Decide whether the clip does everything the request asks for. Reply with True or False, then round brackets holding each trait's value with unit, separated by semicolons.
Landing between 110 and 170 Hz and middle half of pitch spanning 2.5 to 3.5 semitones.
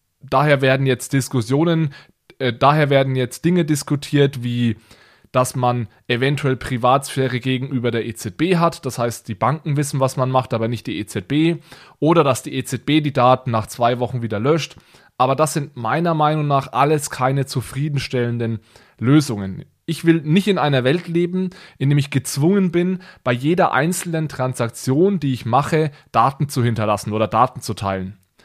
False (135 Hz; 4.1 semitones)